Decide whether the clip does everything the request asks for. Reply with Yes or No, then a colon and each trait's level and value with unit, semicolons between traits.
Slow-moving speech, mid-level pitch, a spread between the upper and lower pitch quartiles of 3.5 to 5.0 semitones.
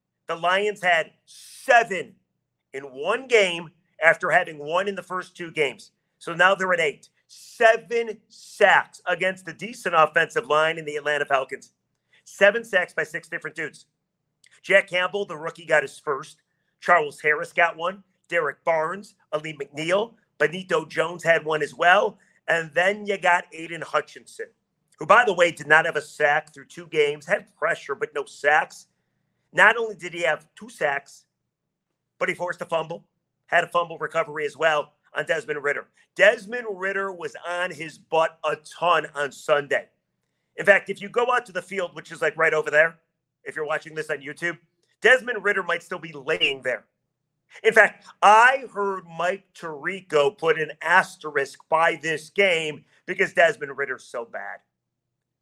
No: average, 170 wpm; medium, 170 Hz; average, 4.0 semitones